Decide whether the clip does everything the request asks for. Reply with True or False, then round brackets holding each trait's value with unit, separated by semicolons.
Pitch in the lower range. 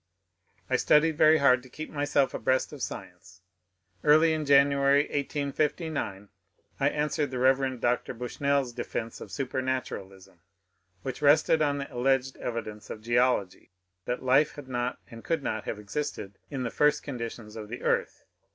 True (130 Hz)